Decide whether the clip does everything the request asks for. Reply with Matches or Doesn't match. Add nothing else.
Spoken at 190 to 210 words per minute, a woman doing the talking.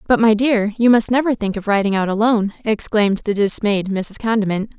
Matches